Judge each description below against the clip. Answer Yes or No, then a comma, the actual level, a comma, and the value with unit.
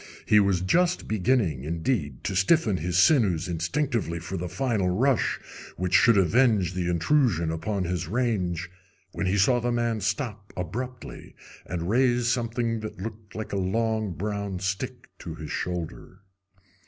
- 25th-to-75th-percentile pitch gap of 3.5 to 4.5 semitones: No, average, 5.0 semitones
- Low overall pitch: Yes, low, 100 Hz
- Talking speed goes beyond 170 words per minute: No, average, 150 wpm